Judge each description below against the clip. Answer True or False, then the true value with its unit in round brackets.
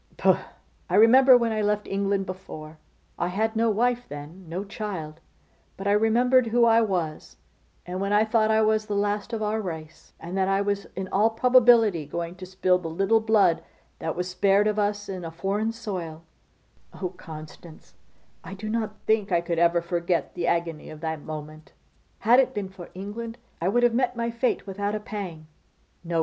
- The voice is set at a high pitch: True (200 Hz)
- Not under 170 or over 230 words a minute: True (190 wpm)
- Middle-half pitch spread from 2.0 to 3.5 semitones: False (4.3 semitones)